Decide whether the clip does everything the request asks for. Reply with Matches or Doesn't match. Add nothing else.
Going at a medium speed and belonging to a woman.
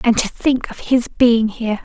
Doesn't match